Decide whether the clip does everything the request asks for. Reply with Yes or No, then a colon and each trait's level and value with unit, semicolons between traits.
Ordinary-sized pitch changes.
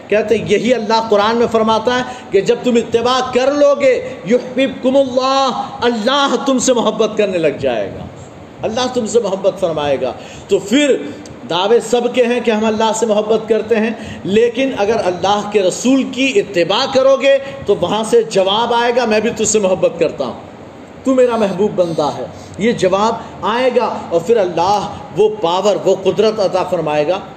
Yes: average, 4.1 semitones